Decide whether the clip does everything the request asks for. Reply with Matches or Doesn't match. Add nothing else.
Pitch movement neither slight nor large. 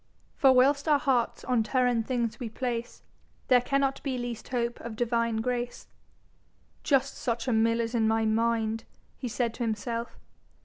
Doesn't match